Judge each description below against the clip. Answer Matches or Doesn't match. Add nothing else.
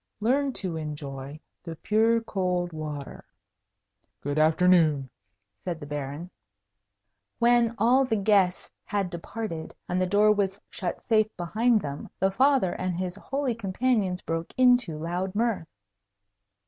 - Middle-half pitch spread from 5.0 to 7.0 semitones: Matches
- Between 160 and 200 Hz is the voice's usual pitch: Matches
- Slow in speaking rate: Matches